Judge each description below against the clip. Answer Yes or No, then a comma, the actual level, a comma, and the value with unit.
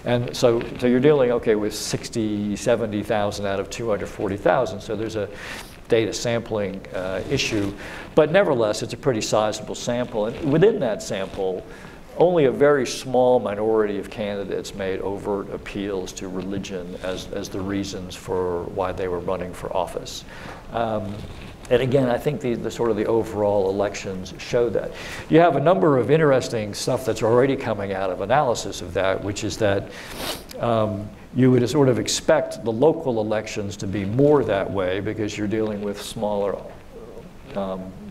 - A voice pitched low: Yes, low, 105 Hz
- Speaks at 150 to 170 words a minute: Yes, average, 165 wpm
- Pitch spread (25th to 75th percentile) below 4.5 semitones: Yes, average, 3.4 semitones